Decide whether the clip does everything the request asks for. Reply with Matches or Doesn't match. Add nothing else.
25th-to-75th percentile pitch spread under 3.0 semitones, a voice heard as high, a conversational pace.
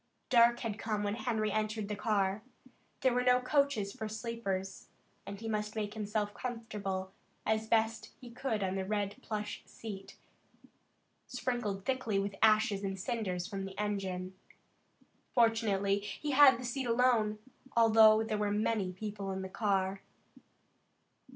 Matches